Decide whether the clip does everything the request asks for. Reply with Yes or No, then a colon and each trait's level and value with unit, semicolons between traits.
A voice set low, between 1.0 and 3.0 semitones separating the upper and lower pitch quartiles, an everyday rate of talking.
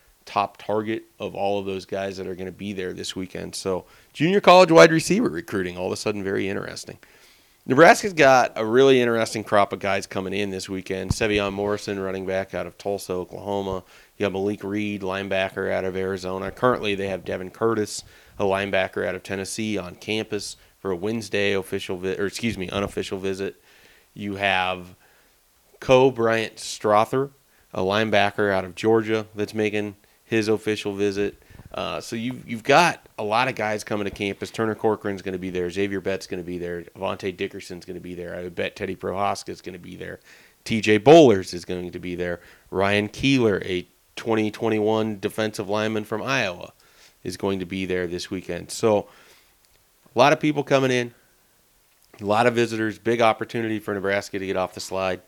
Yes: low, 100 Hz; narrow, 2.6 semitones; average, 190 wpm